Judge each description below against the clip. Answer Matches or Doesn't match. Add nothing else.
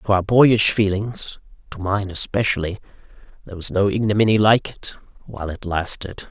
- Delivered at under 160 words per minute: Matches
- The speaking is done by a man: Matches